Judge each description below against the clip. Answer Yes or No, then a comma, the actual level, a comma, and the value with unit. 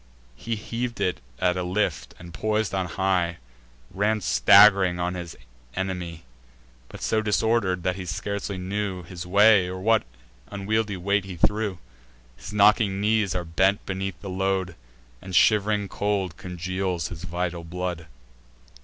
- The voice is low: Yes, very low, 95 Hz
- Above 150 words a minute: No, average, 145 wpm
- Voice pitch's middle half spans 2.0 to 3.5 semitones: Yes, narrow, 2.6 semitones